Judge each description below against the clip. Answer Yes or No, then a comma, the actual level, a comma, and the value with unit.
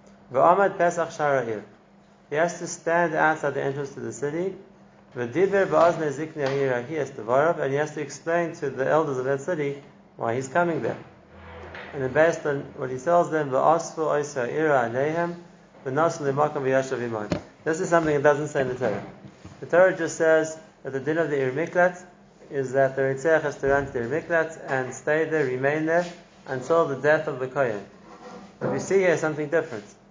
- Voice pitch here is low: No, medium, 155 Hz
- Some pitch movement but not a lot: Yes, average, 3.5 semitones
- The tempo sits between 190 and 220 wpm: No, average, 155 wpm